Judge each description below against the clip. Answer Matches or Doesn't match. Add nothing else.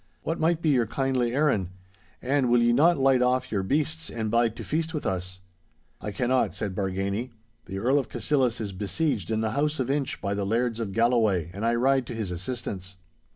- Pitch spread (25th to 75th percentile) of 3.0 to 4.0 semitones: Doesn't match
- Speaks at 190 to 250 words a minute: Matches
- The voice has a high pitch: Doesn't match